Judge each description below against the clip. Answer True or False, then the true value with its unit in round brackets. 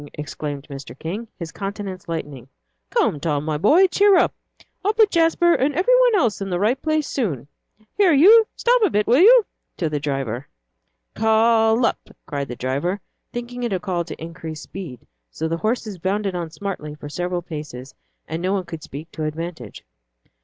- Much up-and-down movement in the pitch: True (8.2 semitones)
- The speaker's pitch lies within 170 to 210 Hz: True (185 Hz)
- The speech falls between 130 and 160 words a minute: False (180 wpm)